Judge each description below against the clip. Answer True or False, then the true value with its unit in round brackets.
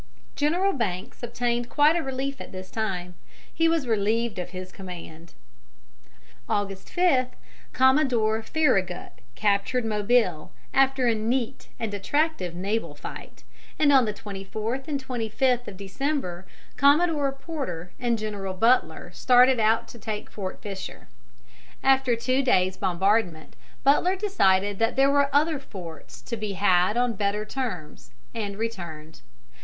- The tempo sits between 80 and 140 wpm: True (135 wpm)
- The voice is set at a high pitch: True (225 Hz)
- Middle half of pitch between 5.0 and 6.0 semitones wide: True (5.6 semitones)